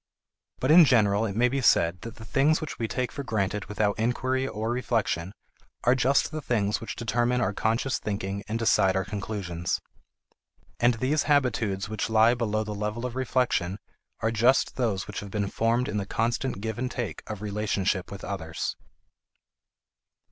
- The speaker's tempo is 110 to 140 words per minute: No, average, 175 wpm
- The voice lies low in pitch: Yes, low, 110 Hz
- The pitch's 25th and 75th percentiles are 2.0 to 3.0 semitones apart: No, average, 3.5 semitones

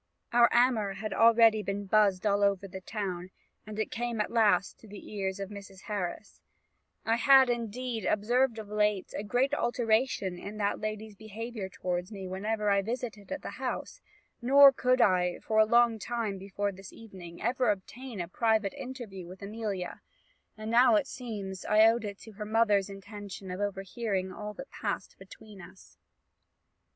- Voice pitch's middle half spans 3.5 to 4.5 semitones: No, average, 2.9 semitones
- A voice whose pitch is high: Yes, high, 210 Hz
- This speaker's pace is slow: No, average, 170 wpm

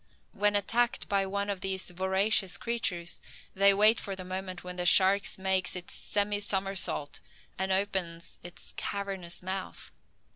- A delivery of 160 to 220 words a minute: No, average, 145 wpm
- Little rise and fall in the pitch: Yes, narrow, 1.6 semitones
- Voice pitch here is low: No, high, 190 Hz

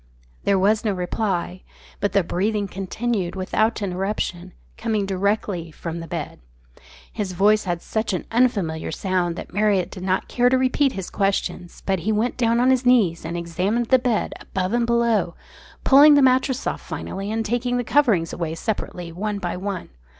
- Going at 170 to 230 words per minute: Yes, average, 175 wpm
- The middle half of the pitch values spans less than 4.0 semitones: No, average, 4.4 semitones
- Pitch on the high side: Yes, high, 200 Hz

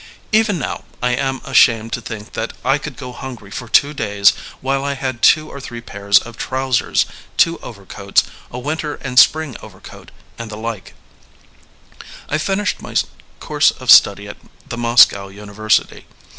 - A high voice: No, low, 125 Hz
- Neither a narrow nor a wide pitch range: Yes, average, 4.4 semitones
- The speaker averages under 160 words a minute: No, average, 165 wpm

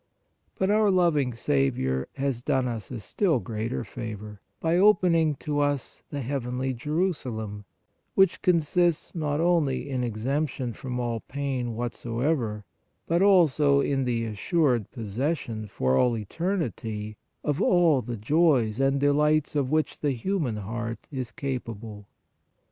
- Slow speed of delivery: Yes, slow, 130 wpm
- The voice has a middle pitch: No, low, 130 Hz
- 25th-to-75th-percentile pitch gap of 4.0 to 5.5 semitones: Yes, average, 5.1 semitones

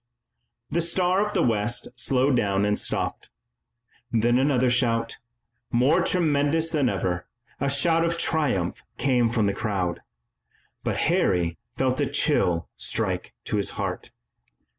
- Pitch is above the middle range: No, low, 125 Hz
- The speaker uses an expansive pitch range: Yes, wide, 6.6 semitones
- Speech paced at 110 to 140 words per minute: Yes, slow, 135 wpm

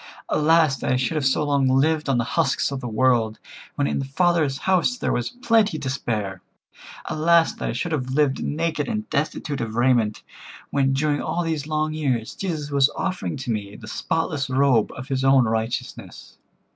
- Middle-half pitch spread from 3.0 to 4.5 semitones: Yes, average, 3.5 semitones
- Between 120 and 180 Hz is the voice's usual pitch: Yes, medium, 140 Hz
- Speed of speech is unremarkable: Yes, average, 195 wpm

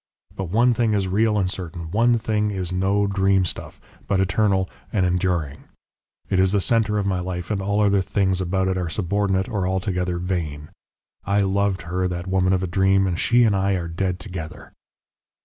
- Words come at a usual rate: Yes, average, 190 wpm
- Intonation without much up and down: Yes, narrow, 1.9 semitones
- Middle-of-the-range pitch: No, very low, 95 Hz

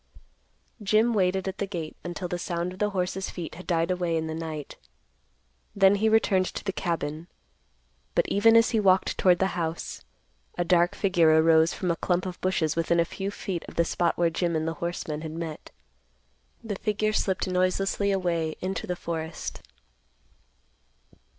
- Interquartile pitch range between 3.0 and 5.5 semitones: No, narrow, 2.6 semitones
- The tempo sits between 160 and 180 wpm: Yes, average, 175 wpm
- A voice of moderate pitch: Yes, medium, 180 Hz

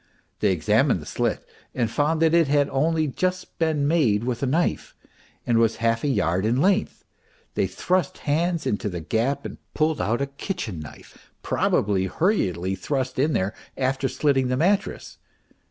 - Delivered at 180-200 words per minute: No, average, 170 wpm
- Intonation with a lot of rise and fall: Yes, wide, 6.0 semitones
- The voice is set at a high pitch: No, low, 135 Hz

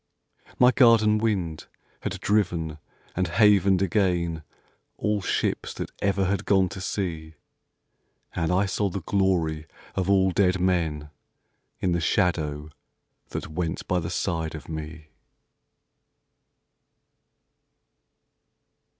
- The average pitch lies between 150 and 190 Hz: No, very low, 90 Hz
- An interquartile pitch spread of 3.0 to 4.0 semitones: Yes, average, 3.5 semitones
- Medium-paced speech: No, slow, 110 wpm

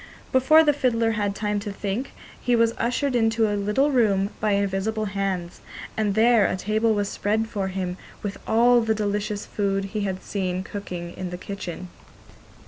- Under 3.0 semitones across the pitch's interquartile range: Yes, narrow, 2.4 semitones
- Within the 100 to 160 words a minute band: No, average, 175 wpm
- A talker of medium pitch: No, high, 210 Hz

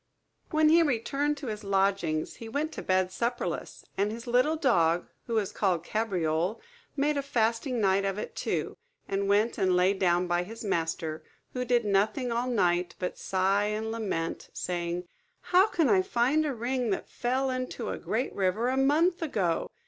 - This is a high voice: Yes, high, 220 Hz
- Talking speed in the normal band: Yes, average, 180 wpm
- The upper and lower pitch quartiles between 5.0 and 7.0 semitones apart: Yes, wide, 5.4 semitones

